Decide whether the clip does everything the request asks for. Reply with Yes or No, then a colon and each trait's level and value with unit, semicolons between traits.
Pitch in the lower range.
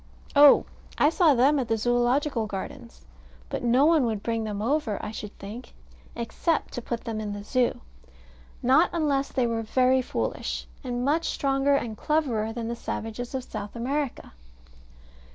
No: high, 245 Hz